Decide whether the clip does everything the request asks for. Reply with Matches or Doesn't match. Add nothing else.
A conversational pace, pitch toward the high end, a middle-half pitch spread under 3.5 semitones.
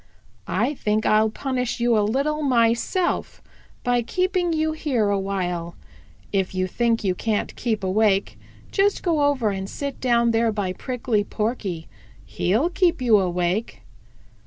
Doesn't match